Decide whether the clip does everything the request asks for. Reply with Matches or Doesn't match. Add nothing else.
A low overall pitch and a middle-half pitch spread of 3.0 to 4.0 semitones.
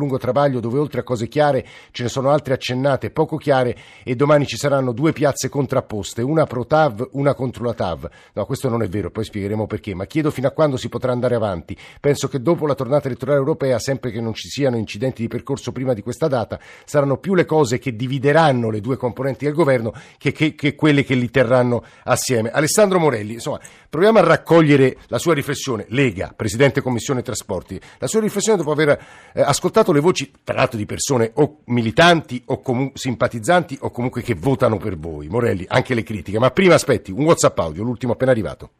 Matches